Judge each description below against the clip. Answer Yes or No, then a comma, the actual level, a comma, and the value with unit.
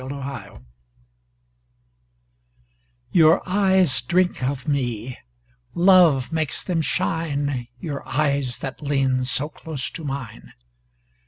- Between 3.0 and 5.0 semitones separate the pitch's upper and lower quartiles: Yes, average, 3.8 semitones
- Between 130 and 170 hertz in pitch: Yes, medium, 140 Hz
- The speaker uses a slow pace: Yes, slow, 100 wpm